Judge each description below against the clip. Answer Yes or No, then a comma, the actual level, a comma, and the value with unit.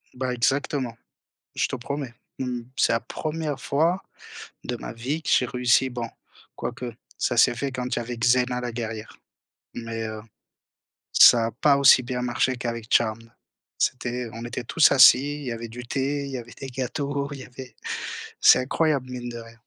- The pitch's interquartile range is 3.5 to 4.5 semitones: No, narrow, 2.4 semitones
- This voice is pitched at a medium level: No, low, 125 Hz